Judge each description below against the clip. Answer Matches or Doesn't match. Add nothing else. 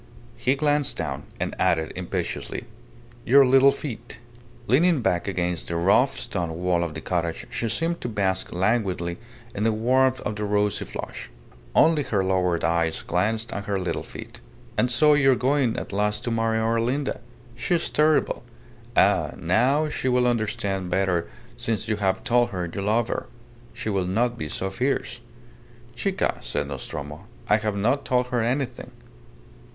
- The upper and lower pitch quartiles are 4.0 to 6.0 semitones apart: Matches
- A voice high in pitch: Doesn't match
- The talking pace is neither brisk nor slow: Matches